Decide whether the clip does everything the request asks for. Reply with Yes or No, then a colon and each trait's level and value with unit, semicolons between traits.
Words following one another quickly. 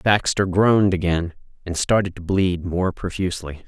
No: average, 145 wpm